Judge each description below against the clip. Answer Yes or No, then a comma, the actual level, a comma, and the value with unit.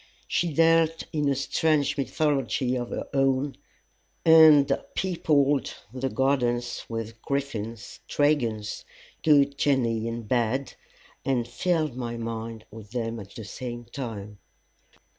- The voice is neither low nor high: No, low, 130 Hz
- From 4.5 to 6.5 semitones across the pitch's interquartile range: No, average, 3.9 semitones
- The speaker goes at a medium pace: No, slow, 120 wpm